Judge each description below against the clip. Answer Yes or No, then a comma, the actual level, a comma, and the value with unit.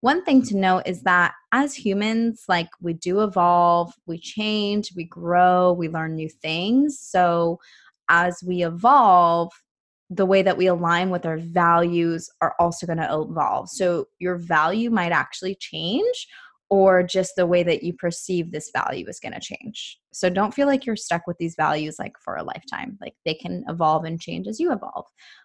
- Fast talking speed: No, average, 185 wpm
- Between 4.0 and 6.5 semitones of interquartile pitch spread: No, average, 3.2 semitones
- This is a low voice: No, medium, 180 Hz